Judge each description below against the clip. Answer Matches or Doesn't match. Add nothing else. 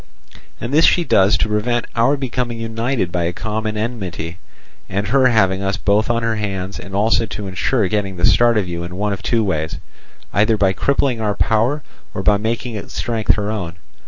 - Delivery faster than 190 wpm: Matches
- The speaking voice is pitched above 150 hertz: Doesn't match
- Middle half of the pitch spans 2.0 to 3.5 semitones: Matches